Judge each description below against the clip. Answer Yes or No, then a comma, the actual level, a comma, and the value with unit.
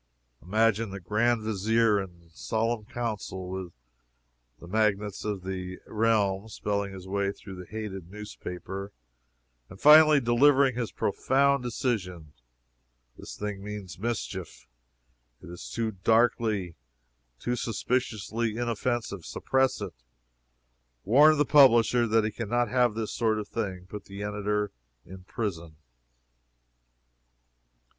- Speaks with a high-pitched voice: No, low, 105 Hz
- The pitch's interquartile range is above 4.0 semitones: No, average, 3.5 semitones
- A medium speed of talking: No, slow, 120 wpm